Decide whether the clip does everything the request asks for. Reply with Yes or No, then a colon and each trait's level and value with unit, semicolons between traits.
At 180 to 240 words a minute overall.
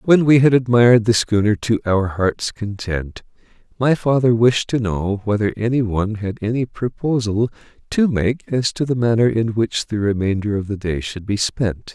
Yes: average, 185 wpm